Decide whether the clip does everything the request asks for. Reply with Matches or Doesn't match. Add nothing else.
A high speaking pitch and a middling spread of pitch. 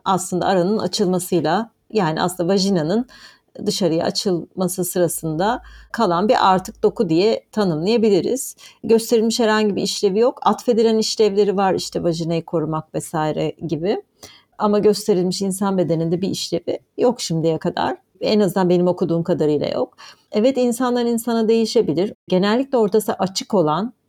Matches